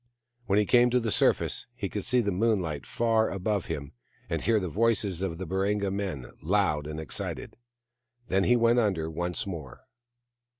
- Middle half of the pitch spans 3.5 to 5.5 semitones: Yes, average, 4.4 semitones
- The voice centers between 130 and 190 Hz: No, low, 100 Hz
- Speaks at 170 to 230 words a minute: Yes, average, 175 wpm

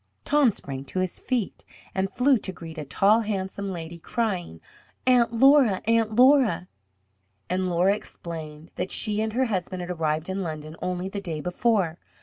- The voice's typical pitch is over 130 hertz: Yes, high, 190 Hz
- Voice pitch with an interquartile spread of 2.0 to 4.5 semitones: No, average, 4.9 semitones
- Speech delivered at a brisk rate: No, average, 165 wpm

